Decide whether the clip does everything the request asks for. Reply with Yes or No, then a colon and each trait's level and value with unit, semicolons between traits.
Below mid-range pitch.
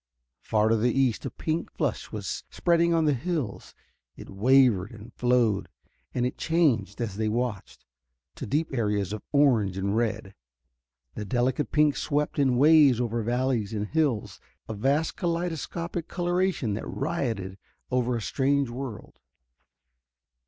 Yes: low, 125 Hz